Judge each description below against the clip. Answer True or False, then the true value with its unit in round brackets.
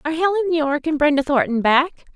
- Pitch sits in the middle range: False (295 Hz)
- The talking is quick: False (195 wpm)